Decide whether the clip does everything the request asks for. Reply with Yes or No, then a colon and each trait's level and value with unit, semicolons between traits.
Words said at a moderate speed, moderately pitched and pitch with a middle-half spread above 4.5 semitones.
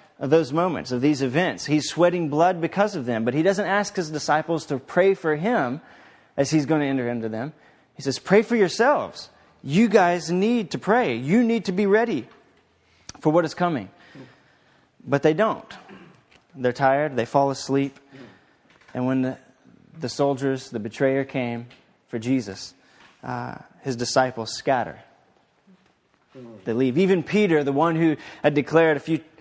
Yes: average, 165 wpm; medium, 150 Hz; average, 5.1 semitones